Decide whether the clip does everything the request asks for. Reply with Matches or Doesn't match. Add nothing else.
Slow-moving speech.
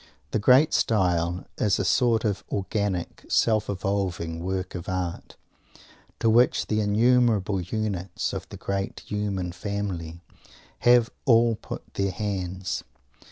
Matches